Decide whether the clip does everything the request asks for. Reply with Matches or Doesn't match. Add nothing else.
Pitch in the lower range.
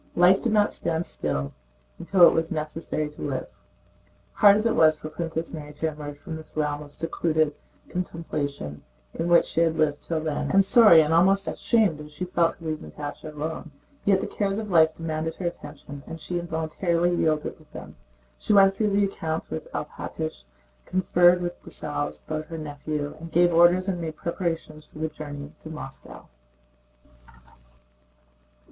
Doesn't match